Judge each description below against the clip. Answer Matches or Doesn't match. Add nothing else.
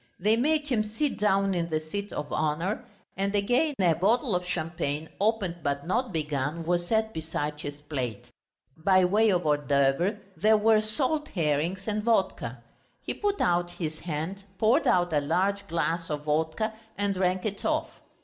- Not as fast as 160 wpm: Doesn't match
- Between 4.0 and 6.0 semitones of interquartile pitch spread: Matches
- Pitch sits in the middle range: Matches